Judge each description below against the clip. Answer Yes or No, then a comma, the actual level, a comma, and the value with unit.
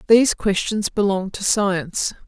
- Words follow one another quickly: No, slow, 130 wpm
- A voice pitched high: Yes, high, 205 Hz